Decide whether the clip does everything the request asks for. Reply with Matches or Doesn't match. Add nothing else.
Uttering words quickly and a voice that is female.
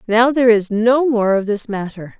Matches